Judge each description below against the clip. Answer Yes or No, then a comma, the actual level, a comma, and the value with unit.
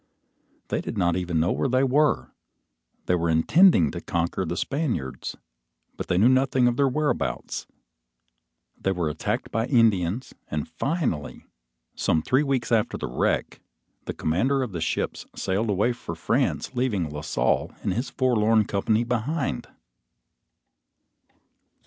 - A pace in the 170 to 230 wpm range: No, average, 145 wpm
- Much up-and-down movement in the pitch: Yes, wide, 7.0 semitones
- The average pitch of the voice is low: Yes, low, 110 Hz